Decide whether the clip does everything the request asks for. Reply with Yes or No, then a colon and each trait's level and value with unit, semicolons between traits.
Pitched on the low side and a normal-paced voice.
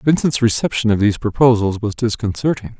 Yes: low, 115 Hz; average, 150 wpm